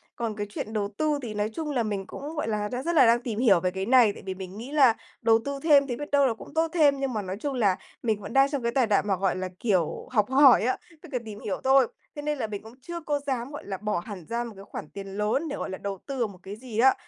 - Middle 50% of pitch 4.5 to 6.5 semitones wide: Yes, average, 5.1 semitones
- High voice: Yes, high, 235 Hz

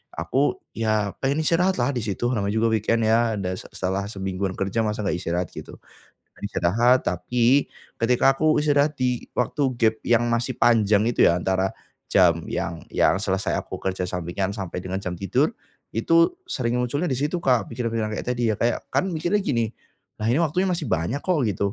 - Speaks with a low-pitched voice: Yes, low, 115 Hz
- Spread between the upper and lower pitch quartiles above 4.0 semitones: Yes, average, 4.8 semitones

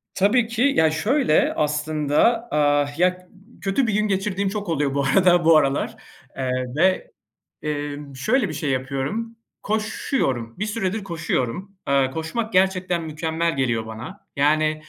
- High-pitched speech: No, medium, 165 Hz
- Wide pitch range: Yes, wide, 5.8 semitones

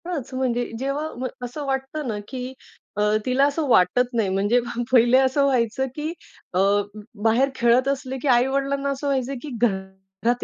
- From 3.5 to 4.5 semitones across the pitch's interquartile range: No, average, 2.7 semitones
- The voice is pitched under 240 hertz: No, very high, 255 Hz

